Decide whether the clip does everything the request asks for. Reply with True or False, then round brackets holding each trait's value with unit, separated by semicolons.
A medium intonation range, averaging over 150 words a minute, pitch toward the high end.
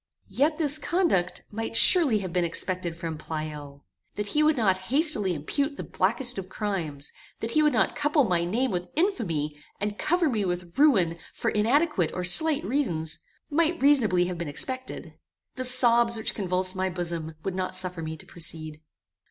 False (7.9 semitones; 175 wpm; 195 Hz)